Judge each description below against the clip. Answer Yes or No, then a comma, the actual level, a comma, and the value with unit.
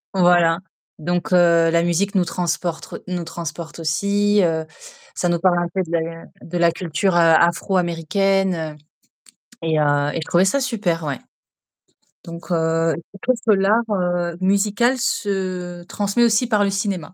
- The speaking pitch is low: No, medium, 175 Hz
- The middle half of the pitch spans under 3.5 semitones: Yes, average, 2.9 semitones